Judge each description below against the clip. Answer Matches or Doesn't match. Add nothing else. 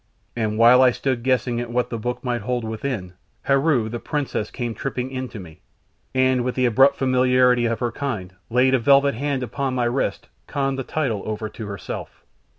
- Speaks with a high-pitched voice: Doesn't match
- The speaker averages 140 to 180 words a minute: Doesn't match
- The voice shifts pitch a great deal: Doesn't match